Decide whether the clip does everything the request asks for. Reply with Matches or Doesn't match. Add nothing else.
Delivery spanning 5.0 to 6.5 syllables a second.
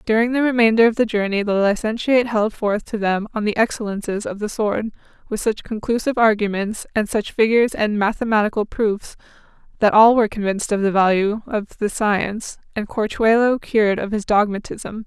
Matches